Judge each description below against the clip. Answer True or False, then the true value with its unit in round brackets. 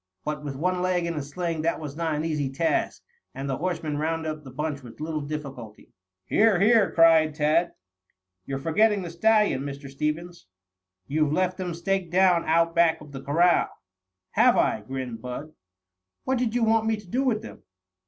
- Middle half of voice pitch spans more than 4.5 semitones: False (3.8 semitones)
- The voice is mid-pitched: True (160 Hz)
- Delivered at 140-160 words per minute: False (185 wpm)